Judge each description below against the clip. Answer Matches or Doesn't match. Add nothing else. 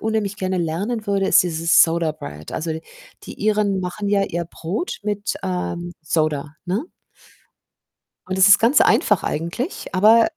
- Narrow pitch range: Doesn't match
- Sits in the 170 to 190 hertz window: Matches